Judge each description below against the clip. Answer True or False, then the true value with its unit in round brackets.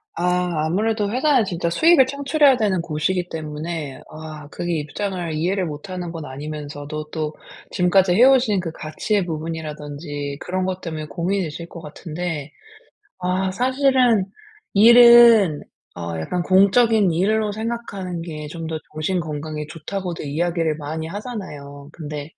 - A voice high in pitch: False (175 Hz)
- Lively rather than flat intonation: False (4.6 semitones)